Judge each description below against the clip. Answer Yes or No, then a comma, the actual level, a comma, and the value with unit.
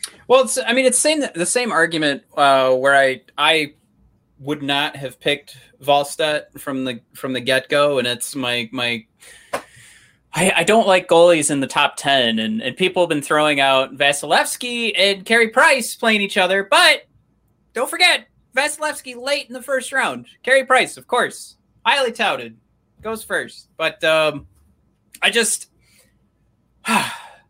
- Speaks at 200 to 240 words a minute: No, average, 155 wpm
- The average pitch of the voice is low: No, medium, 160 Hz